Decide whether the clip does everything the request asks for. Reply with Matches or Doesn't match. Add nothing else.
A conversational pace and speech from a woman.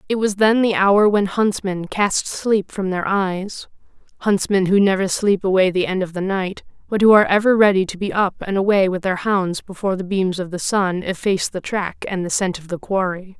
Doesn't match